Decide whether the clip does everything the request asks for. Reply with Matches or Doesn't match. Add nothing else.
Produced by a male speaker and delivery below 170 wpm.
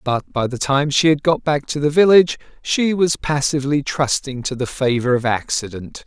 Doesn't match